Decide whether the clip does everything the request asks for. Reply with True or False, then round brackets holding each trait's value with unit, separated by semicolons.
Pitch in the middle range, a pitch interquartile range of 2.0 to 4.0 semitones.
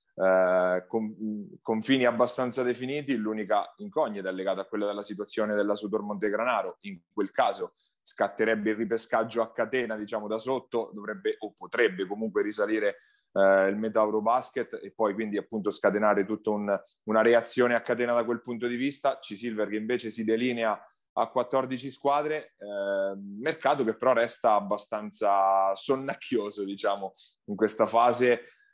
False (110 Hz; 3.2 semitones)